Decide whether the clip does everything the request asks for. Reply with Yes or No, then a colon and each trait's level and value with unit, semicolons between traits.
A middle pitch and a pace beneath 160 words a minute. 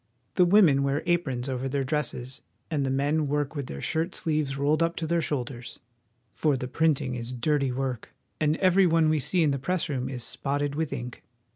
No: medium, 145 Hz; average, 200 wpm